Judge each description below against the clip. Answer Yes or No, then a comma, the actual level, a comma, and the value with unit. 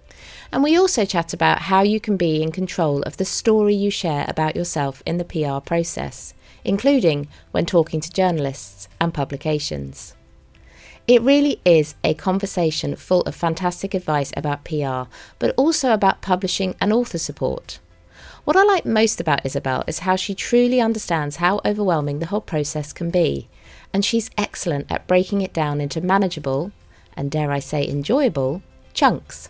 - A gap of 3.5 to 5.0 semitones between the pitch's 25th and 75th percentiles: No, wide, 5.5 semitones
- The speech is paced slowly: No, average, 165 wpm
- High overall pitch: No, medium, 170 Hz